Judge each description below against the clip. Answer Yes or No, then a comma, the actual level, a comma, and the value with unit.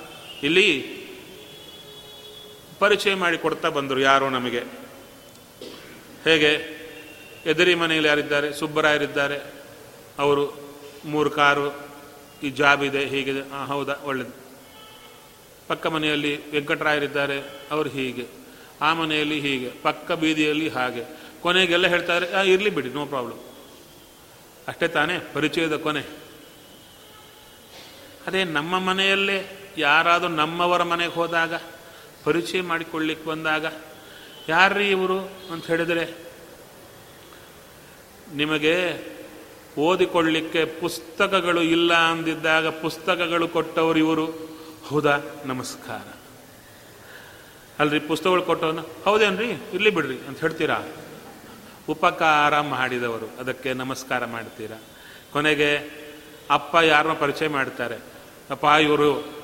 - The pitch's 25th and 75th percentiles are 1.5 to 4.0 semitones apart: Yes, average, 2.7 semitones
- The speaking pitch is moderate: Yes, medium, 155 Hz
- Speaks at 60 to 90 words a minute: Yes, average, 85 wpm